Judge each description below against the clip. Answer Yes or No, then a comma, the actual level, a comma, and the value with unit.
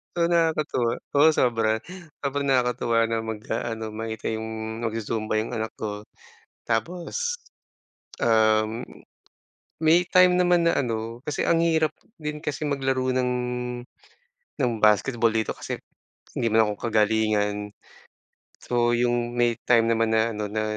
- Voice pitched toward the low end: Yes, low, 115 Hz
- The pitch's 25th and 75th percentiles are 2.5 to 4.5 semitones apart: Yes, average, 4.1 semitones